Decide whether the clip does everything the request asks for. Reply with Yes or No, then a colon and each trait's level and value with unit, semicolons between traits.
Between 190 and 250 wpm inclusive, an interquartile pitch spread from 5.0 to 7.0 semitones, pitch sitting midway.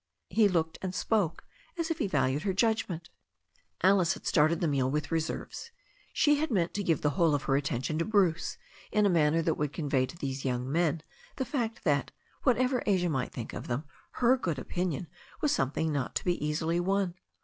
Yes: fast, 205 wpm; wide, 5.4 semitones; medium, 165 Hz